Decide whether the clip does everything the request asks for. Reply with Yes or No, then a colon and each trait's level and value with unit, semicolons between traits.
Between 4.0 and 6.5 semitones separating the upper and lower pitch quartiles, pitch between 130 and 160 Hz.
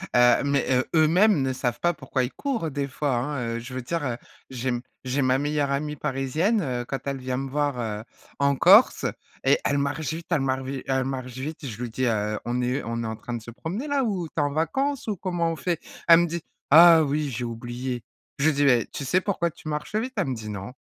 Yes: average, 4.6 semitones; medium, 140 Hz